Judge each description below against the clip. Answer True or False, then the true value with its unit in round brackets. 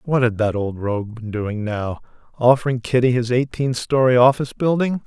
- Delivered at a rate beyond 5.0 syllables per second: True (5.3 syllables/s)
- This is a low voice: True (120 Hz)